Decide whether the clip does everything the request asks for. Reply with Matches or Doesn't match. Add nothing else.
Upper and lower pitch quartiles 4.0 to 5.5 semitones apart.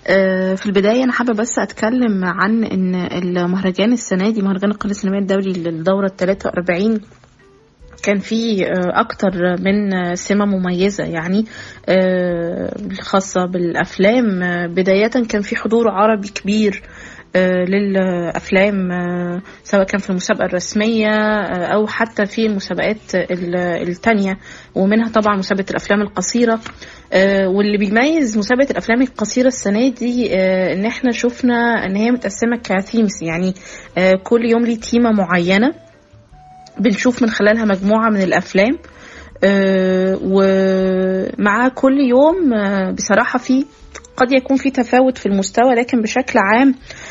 Doesn't match